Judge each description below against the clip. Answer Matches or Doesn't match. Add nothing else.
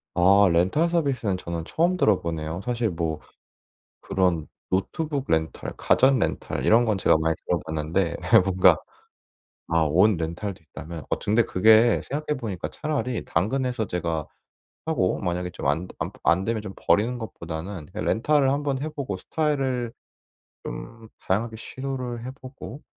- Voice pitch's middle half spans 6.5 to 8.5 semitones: Matches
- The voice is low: Matches